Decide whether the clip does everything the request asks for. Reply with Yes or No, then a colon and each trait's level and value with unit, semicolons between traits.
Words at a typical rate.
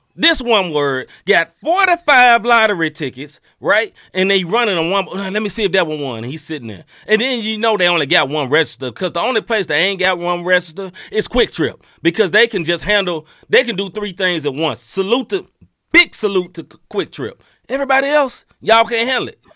No: fast, 220 wpm